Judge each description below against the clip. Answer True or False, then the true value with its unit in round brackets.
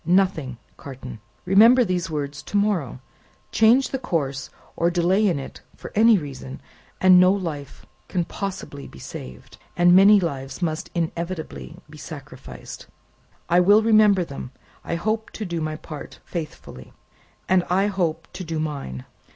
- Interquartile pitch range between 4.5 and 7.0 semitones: True (5.2 semitones)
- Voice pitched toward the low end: False (175 Hz)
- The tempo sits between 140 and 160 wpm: True (150 wpm)